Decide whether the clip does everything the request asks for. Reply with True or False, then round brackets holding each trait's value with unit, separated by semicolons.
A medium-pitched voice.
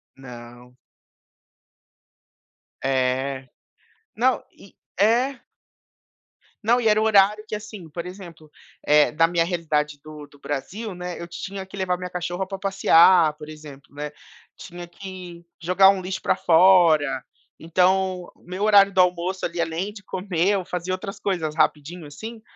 True (180 Hz)